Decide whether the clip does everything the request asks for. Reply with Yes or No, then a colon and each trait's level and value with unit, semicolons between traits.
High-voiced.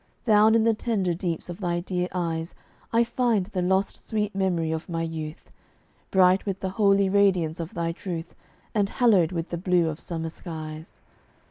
No: medium, 180 Hz